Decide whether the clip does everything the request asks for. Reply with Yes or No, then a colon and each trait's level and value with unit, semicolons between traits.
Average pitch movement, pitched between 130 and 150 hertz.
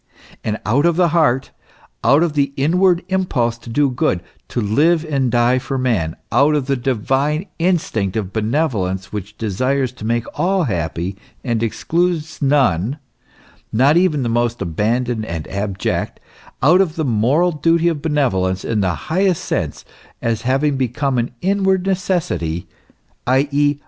No: wide, 6.3 semitones; low, 135 Hz